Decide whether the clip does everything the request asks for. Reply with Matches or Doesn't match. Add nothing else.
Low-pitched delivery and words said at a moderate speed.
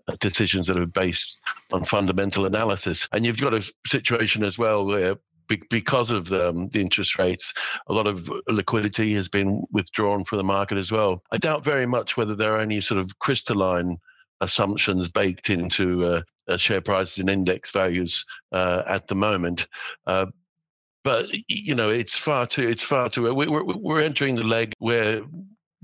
Matches